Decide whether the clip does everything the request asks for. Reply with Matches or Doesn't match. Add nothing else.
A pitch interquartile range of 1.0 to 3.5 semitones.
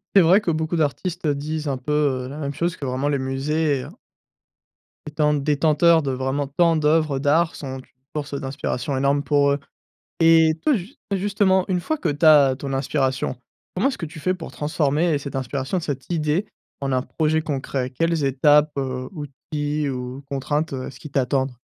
Matches